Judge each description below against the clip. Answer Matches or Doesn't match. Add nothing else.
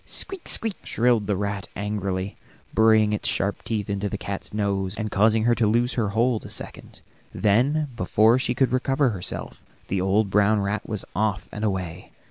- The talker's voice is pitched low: Matches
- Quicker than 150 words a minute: Matches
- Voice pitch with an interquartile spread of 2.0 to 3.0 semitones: Matches